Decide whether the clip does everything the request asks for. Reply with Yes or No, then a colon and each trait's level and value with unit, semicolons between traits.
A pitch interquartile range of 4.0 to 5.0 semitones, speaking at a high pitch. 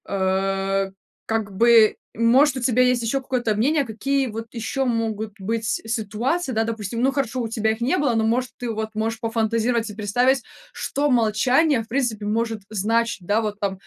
No: narrow, 2.6 semitones; high, 225 Hz